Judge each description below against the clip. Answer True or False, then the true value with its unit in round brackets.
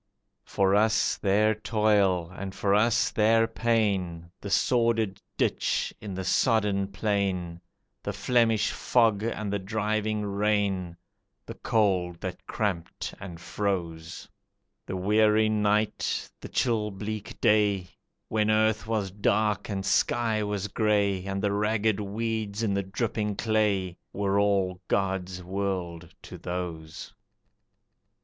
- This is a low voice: True (100 Hz)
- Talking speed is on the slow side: True (125 wpm)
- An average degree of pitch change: False (2.2 semitones)